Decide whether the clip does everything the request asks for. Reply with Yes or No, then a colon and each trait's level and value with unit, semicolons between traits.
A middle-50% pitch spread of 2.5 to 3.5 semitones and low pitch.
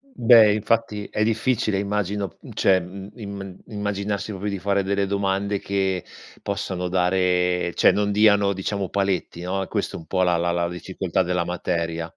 No: narrow, 2.1 semitones; very low, 95 Hz